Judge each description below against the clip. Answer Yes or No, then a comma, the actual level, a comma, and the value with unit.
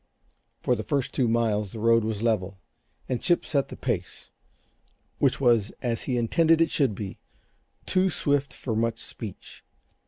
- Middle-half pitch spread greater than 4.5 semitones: No, average, 4.1 semitones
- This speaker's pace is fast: No, average, 160 wpm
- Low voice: Yes, low, 115 Hz